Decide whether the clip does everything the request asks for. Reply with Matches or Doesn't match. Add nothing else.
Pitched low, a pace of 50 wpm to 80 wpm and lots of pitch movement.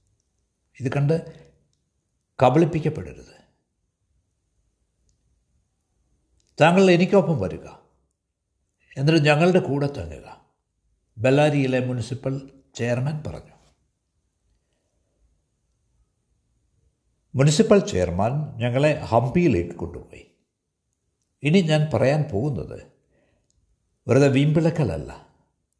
Matches